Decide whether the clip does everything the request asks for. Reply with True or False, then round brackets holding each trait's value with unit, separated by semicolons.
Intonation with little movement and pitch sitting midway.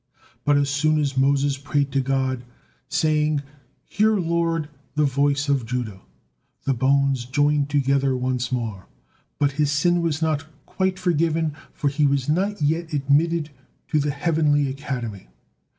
True (2.3 semitones; 145 Hz)